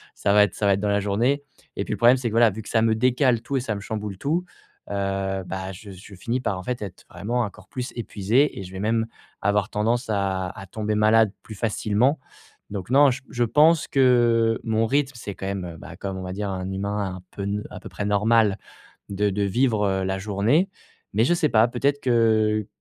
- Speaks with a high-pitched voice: No, low, 105 Hz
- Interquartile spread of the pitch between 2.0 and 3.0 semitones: No, average, 3.4 semitones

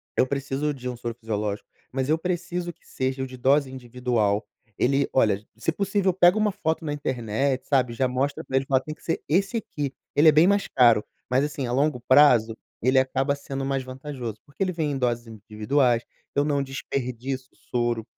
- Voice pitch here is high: No, low, 135 Hz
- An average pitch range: Yes, average, 3.2 semitones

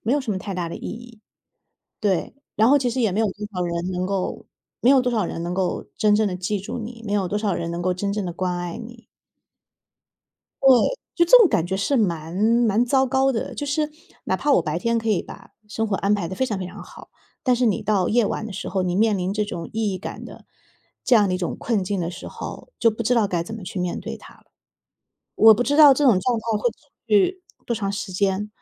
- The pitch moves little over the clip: No, average, 4.3 semitones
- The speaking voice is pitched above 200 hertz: Yes, high, 210 Hz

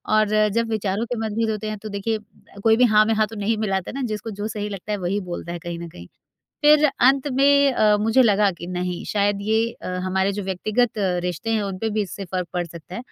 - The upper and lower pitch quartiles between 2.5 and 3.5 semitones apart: Yes, average, 2.9 semitones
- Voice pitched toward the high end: Yes, high, 210 Hz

